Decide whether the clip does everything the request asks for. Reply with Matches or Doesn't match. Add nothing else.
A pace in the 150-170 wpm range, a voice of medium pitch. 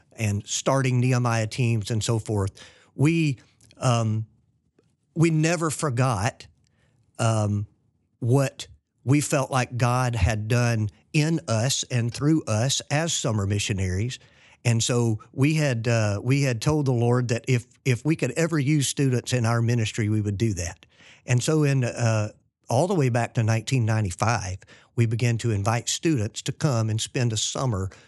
Doesn't match